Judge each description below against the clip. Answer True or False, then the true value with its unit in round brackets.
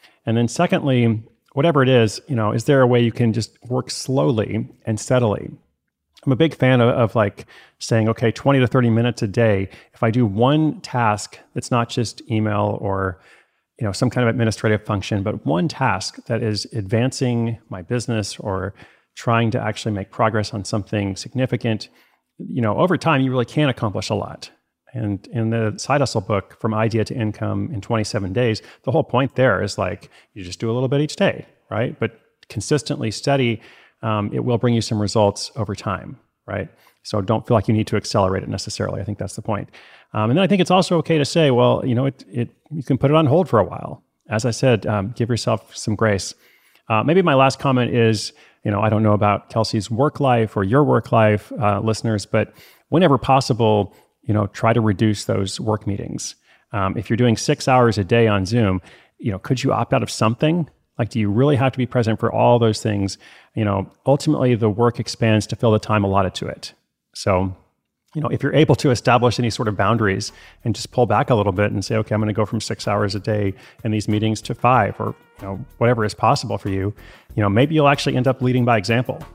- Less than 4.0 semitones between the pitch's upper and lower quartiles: True (3.1 semitones)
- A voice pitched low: True (115 Hz)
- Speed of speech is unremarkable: False (225 wpm)